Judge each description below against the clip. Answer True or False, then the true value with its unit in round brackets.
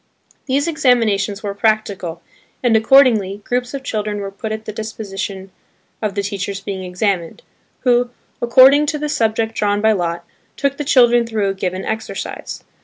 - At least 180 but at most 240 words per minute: False (160 wpm)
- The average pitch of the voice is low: False (215 Hz)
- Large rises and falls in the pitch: False (3.6 semitones)